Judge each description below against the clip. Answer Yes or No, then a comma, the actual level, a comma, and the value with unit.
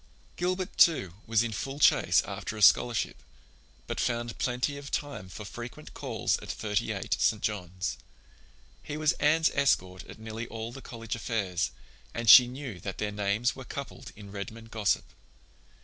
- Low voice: Yes, low, 115 Hz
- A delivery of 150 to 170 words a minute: Yes, average, 165 wpm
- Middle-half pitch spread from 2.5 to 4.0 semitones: No, average, 4.4 semitones